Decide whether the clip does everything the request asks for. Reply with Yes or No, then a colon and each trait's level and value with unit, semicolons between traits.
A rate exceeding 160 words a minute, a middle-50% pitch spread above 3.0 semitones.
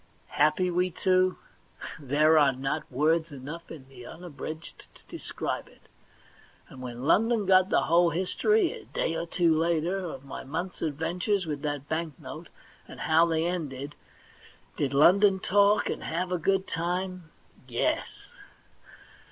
No: average, 145 wpm; average, 3.7 semitones